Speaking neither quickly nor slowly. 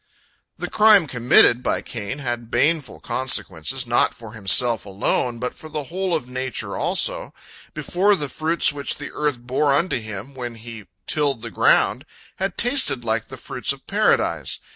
Yes: average, 165 wpm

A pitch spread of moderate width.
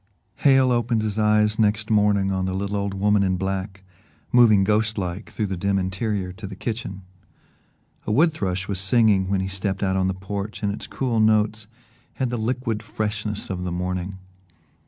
No: narrow, 2.3 semitones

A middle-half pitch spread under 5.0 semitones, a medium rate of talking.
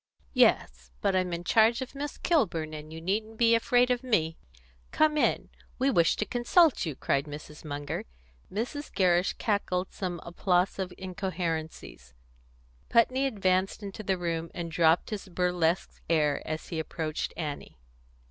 No: wide, 5.4 semitones; average, 150 wpm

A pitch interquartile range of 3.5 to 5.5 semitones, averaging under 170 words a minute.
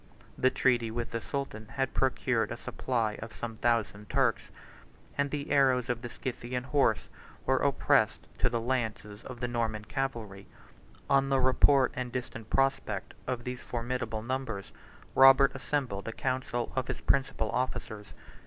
No: average, 2.7 semitones; average, 155 wpm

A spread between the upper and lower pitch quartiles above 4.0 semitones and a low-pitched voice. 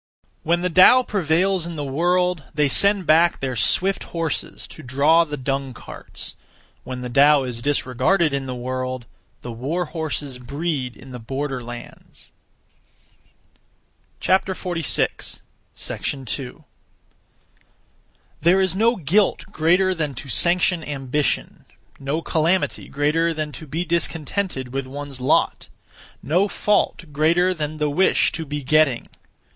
No: average, 4.4 semitones; medium, 150 Hz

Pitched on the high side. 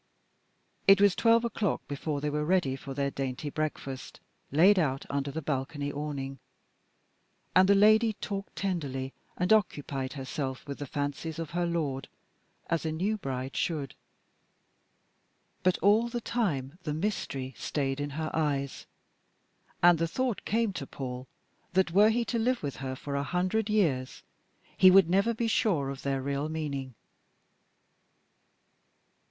No: medium, 155 Hz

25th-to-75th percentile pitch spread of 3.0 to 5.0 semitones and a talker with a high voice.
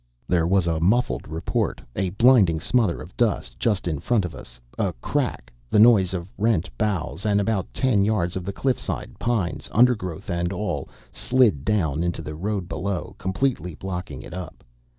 No: average, 4.2 semitones; very low, 95 Hz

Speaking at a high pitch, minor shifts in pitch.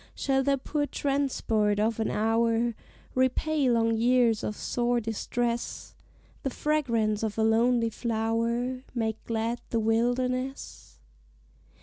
Yes: high, 235 Hz; narrow, 2.2 semitones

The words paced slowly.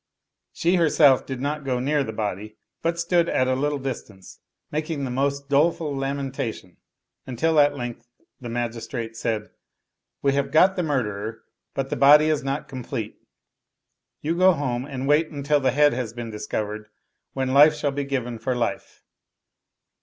No: average, 165 wpm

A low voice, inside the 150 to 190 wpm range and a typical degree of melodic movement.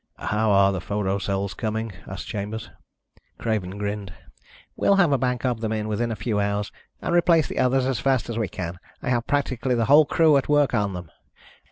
No: low, 110 Hz; fast, 205 wpm; average, 4.2 semitones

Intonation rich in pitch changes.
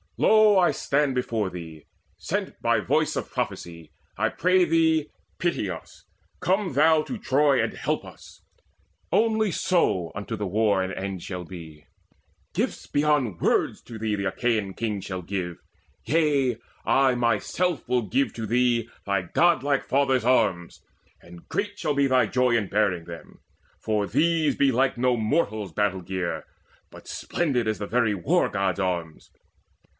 Yes: wide, 7.1 semitones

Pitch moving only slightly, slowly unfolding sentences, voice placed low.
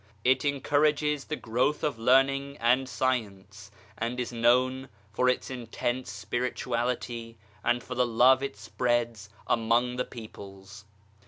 Yes: narrow, 2.3 semitones; slow, 130 wpm; low, 125 Hz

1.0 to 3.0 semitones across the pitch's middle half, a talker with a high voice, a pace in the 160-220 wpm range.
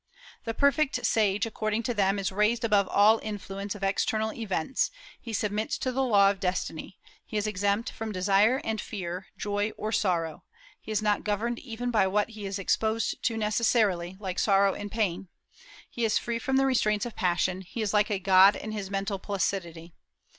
Yes: narrow, 2.4 semitones; high, 210 Hz; average, 190 wpm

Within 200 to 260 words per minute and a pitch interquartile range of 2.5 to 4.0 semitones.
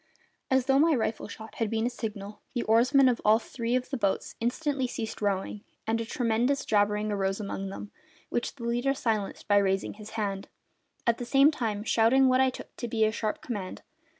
Yes: fast, 205 wpm; average, 3.3 semitones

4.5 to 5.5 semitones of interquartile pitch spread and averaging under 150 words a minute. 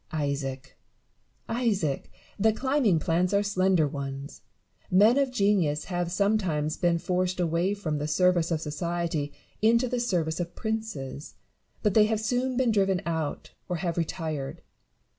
Yes: average, 5.1 semitones; average, 140 wpm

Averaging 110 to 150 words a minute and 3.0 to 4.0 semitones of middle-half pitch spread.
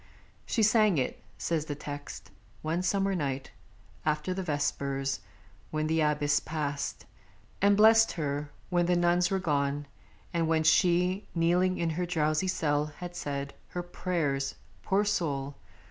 Yes: average, 145 wpm; average, 3.7 semitones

